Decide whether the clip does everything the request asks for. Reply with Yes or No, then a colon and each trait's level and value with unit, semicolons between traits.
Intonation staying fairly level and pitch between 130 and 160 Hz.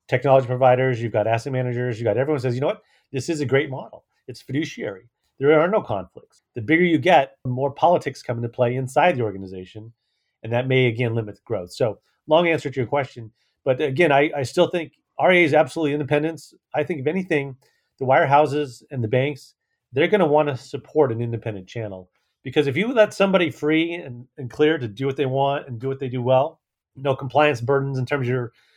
No: average, 3.5 semitones; low, 135 Hz